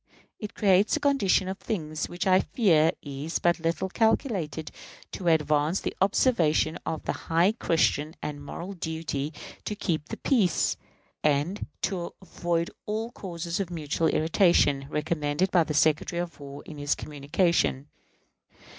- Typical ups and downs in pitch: Yes, average, 3.9 semitones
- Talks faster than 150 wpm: No, average, 145 wpm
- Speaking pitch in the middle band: Yes, medium, 165 Hz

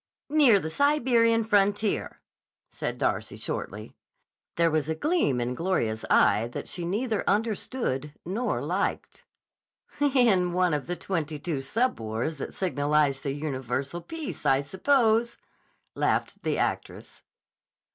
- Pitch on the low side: No, medium, 180 Hz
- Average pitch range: No, wide, 8.1 semitones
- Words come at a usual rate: No, slow, 125 wpm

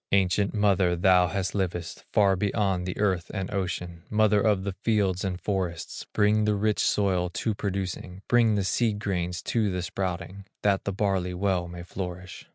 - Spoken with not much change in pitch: Yes, narrow, 2.2 semitones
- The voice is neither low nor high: No, very low, 95 Hz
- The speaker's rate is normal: Yes, average, 170 wpm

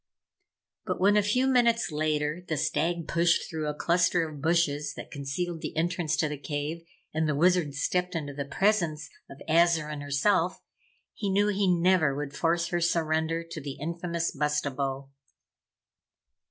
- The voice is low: No, medium, 165 Hz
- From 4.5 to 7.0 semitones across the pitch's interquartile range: No, average, 2.9 semitones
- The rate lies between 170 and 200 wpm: No, average, 155 wpm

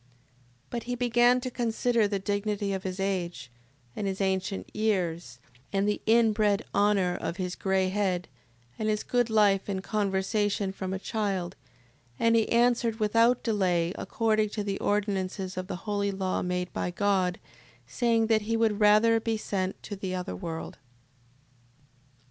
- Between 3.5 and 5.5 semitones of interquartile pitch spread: No, average, 2.7 semitones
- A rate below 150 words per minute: No, average, 160 wpm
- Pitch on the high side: Yes, high, 205 Hz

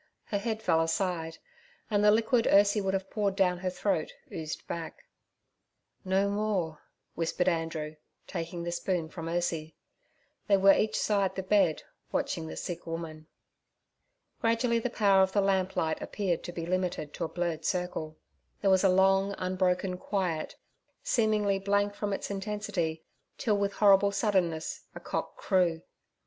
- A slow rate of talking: No, average, 155 wpm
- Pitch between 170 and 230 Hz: Yes, high, 190 Hz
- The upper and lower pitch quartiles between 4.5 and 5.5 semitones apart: No, average, 3.3 semitones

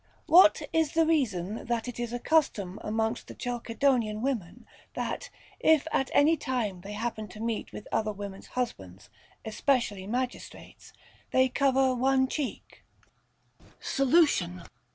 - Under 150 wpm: Yes, slow, 135 wpm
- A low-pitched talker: No, high, 240 Hz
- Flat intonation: No, average, 4.2 semitones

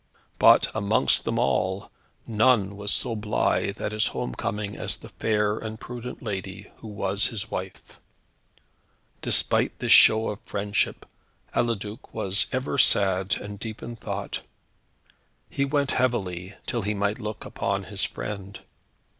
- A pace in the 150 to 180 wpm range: No, average, 140 wpm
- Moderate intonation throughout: No, narrow, 2.1 semitones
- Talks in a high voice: No, low, 105 Hz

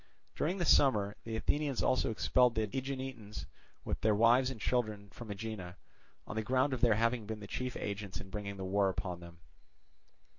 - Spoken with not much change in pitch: No, average, 3.9 semitones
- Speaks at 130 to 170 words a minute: No, average, 185 wpm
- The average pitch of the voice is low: Yes, low, 110 Hz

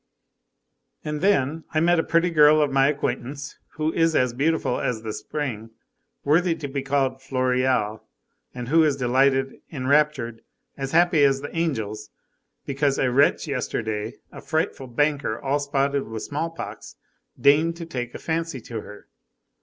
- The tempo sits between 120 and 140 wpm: No, average, 160 wpm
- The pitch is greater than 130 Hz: Yes, medium, 140 Hz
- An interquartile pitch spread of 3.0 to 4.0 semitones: Yes, average, 3.5 semitones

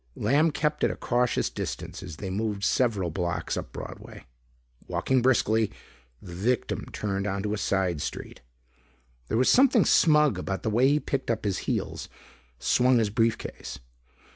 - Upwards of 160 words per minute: No, average, 155 wpm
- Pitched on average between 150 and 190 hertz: No, low, 110 Hz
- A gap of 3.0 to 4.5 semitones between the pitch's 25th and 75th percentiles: No, average, 4.9 semitones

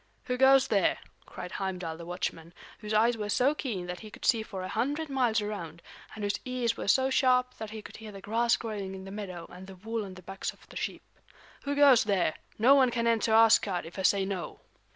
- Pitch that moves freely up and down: No, average, 4.2 semitones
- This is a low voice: No, high, 215 Hz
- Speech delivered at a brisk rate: Yes, fast, 235 wpm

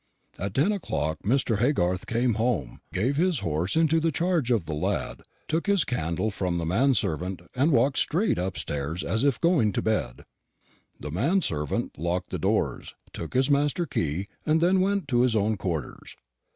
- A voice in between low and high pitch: No, low, 115 Hz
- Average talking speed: Yes, average, 180 wpm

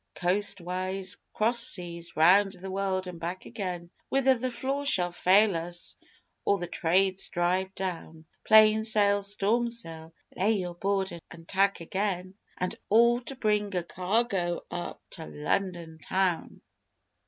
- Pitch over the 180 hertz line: Yes, high, 190 Hz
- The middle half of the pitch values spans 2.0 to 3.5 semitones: Yes, average, 3.1 semitones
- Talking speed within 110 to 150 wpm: Yes, average, 140 wpm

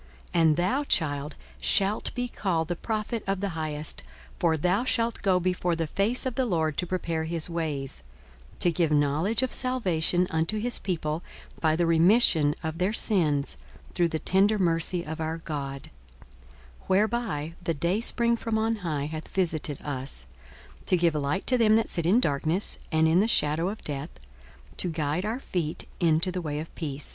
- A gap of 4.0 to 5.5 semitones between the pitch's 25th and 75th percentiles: Yes, average, 4.3 semitones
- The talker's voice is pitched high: No, medium, 170 Hz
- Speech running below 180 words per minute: No, average, 185 wpm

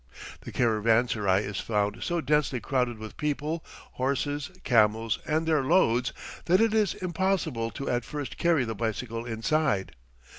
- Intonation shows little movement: No, wide, 5.4 semitones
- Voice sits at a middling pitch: No, low, 125 Hz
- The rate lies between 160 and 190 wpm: No, average, 145 wpm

